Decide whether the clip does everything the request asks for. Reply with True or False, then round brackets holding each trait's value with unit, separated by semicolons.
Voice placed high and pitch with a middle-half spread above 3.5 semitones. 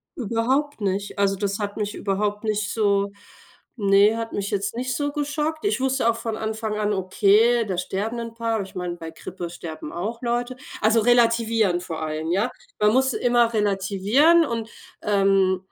False (215 Hz; 3.2 semitones)